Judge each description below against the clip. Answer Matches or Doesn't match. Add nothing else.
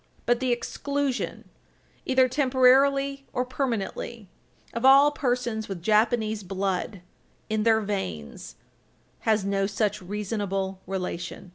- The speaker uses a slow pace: Matches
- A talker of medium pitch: Doesn't match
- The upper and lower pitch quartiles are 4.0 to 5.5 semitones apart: Matches